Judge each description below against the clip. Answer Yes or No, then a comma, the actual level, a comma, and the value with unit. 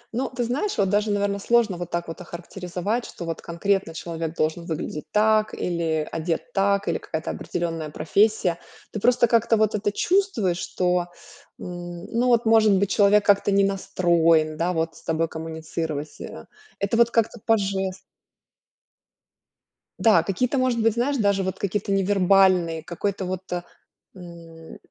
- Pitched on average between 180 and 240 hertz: Yes, high, 190 Hz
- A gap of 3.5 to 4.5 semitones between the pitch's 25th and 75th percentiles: Yes, average, 3.9 semitones